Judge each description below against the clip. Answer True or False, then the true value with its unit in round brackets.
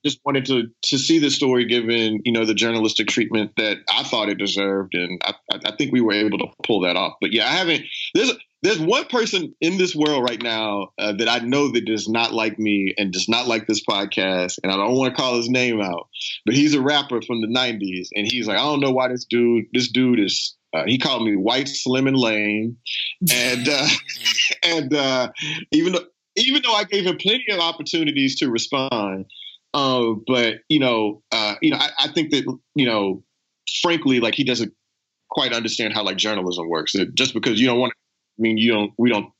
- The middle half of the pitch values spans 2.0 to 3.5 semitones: False (4.3 semitones)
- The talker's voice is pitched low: True (120 Hz)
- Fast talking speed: True (220 wpm)